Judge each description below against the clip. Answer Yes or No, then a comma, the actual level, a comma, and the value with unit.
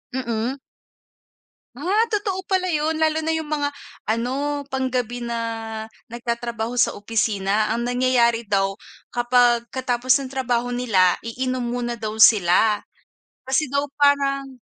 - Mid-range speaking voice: No, high, 245 Hz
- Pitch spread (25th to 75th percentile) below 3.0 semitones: No, average, 3.4 semitones